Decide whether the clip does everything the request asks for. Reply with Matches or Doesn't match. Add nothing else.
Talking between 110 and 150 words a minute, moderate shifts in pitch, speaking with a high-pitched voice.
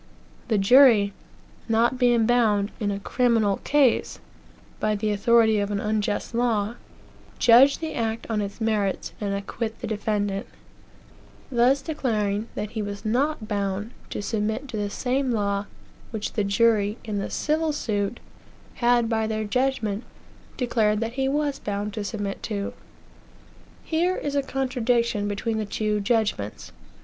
Matches